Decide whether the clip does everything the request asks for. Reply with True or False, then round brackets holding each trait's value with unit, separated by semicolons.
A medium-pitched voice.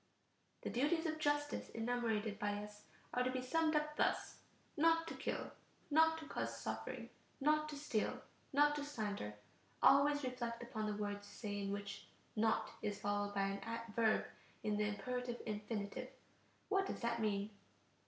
False (235 Hz)